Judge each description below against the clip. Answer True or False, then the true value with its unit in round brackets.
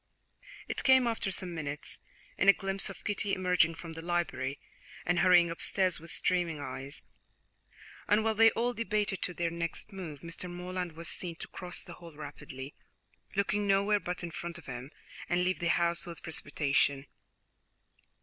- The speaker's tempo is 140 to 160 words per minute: False (170 wpm)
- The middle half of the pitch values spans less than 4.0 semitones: True (3.0 semitones)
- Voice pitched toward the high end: False (175 Hz)